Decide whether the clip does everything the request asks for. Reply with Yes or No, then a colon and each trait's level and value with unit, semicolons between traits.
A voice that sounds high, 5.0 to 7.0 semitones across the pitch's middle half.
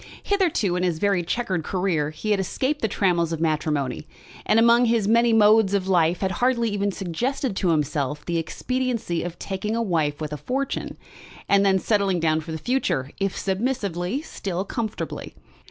Yes: high, 195 Hz; wide, 5.5 semitones